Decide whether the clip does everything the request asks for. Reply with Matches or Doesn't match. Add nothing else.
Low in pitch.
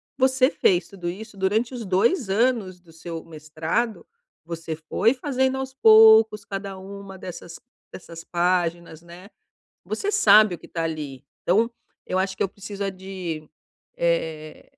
Doesn't match